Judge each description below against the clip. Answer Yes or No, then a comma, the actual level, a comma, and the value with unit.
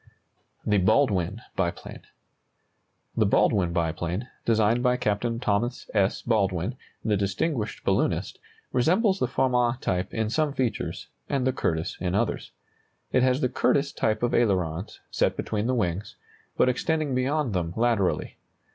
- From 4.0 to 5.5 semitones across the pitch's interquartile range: Yes, average, 4.7 semitones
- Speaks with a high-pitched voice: No, low, 115 Hz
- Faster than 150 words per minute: No, average, 140 wpm